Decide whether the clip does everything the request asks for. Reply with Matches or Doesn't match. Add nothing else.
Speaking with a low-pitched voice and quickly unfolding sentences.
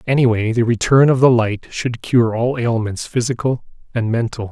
Doesn't match